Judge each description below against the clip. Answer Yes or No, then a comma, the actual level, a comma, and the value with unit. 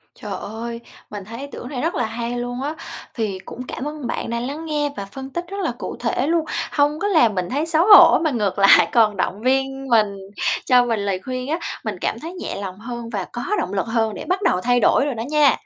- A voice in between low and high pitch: No, high, 245 Hz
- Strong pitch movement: No, average, 5.0 semitones